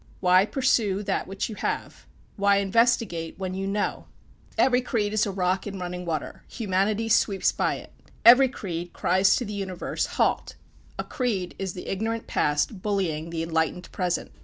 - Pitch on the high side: Yes, high, 195 Hz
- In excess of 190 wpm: No, average, 165 wpm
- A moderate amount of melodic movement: Yes, average, 3.1 semitones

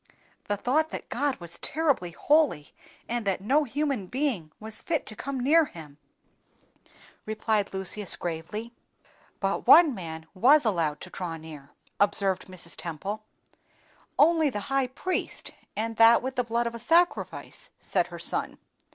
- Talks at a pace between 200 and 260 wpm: No, average, 150 wpm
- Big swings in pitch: Yes, wide, 7.1 semitones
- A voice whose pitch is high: Yes, high, 220 Hz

